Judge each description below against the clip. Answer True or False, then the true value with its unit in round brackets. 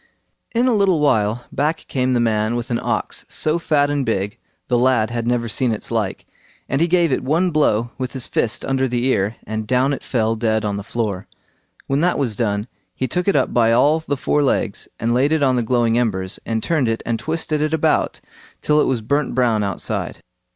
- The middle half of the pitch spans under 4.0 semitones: False (4.4 semitones)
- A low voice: True (125 Hz)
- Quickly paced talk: True (220 wpm)